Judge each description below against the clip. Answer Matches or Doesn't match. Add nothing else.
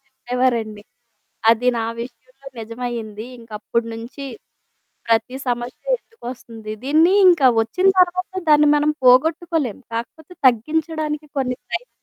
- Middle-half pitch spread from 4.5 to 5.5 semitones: Matches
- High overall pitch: Matches